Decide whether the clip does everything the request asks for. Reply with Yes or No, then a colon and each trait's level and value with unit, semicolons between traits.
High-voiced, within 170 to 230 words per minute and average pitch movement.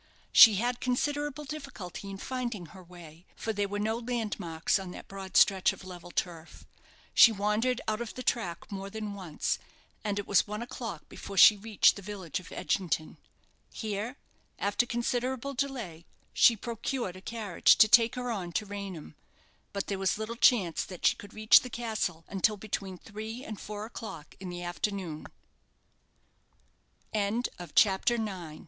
Yes: high, 205 Hz; average, 175 wpm; average, 3.8 semitones